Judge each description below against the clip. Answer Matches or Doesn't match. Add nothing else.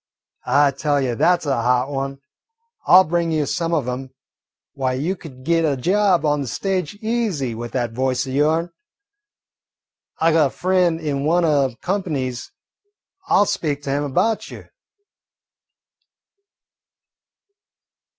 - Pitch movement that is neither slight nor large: Matches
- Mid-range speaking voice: Matches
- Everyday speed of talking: Matches